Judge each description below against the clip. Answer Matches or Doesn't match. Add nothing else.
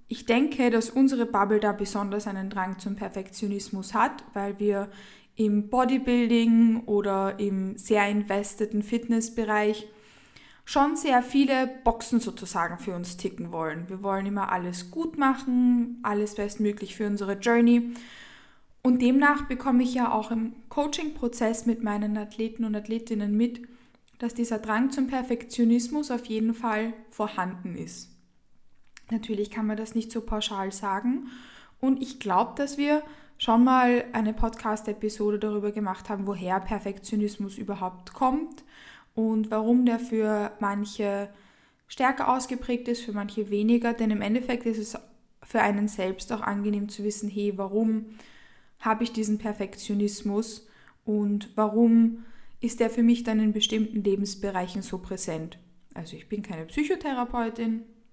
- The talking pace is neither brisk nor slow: Matches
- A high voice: Matches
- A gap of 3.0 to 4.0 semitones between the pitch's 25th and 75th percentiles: Doesn't match